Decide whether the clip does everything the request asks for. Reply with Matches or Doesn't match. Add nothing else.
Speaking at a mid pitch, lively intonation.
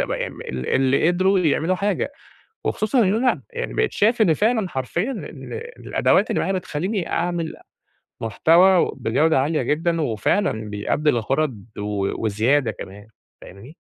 Matches